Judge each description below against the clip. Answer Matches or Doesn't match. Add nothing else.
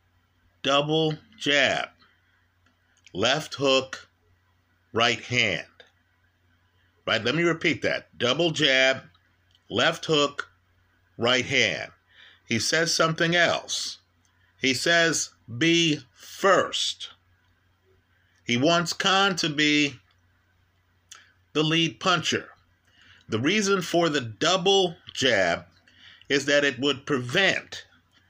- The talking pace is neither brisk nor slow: Doesn't match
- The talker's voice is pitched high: Doesn't match